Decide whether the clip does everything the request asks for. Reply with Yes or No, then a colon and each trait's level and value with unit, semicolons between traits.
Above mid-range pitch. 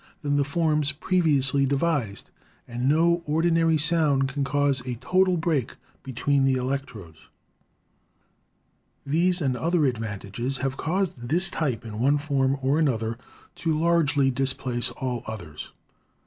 No: medium, 140 Hz